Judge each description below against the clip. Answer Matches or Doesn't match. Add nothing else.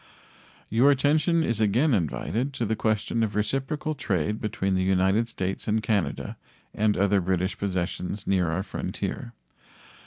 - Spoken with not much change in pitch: Doesn't match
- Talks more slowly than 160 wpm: Matches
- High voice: Doesn't match